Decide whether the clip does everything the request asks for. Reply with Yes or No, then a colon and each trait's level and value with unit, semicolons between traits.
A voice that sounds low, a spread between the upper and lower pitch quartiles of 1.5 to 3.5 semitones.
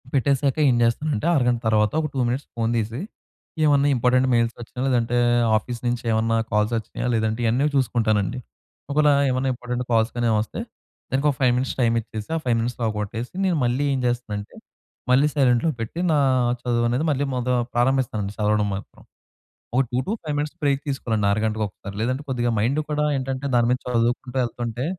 Yes: low, 120 Hz; average, 2.8 semitones